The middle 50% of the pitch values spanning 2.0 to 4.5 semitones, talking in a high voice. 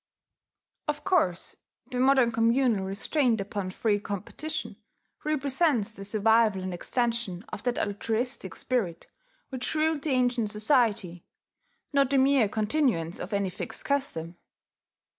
No: average, 5.1 semitones; high, 230 Hz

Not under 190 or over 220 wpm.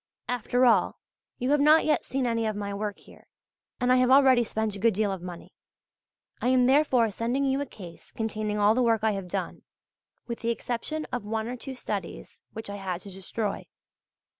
Yes: fast, 205 wpm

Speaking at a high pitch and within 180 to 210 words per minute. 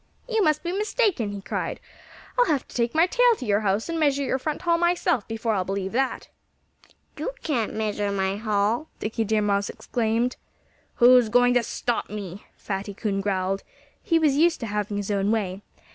Yes: high, 225 Hz; average, 190 wpm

